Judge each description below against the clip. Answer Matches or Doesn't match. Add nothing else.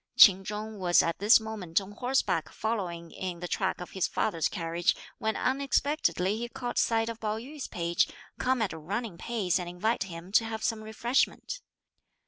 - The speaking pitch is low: Doesn't match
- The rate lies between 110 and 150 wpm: Doesn't match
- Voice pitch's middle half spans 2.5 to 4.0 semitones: Doesn't match